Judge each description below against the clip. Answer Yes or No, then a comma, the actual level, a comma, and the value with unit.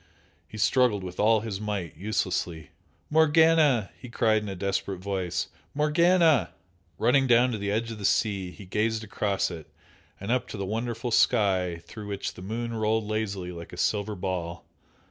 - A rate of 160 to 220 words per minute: Yes, average, 170 wpm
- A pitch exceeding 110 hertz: No, low, 105 Hz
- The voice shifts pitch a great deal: No, average, 3.5 semitones